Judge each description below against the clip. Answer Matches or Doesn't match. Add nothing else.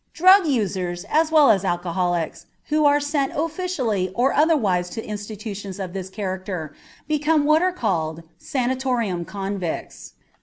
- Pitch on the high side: Matches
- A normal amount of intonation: Doesn't match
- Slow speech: Matches